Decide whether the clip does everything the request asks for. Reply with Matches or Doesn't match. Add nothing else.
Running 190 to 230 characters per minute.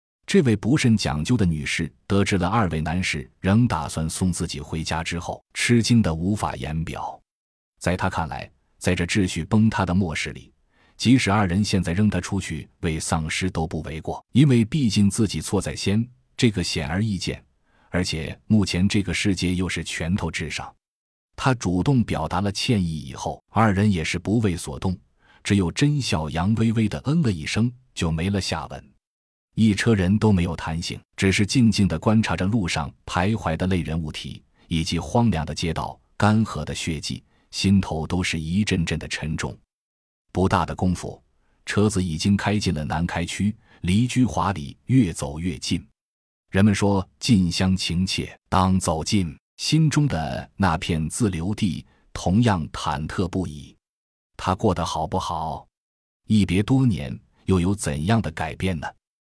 Doesn't match